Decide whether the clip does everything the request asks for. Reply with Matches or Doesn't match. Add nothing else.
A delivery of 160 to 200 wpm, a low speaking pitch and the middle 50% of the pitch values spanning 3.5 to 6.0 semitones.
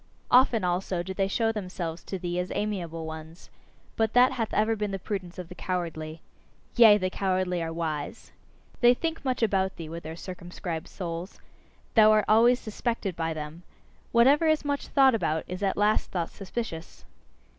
Doesn't match